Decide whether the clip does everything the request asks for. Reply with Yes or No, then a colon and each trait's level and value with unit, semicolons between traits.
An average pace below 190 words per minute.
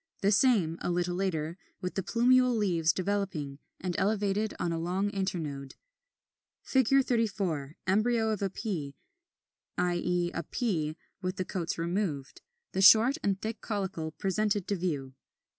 Yes: average, 145 wpm